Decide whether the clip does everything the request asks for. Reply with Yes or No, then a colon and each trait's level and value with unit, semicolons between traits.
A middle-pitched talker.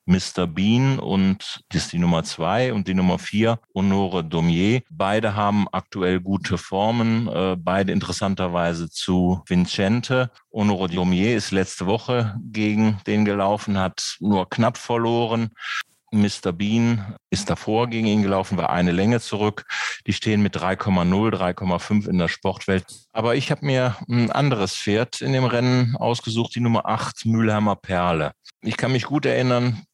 No: low, 105 Hz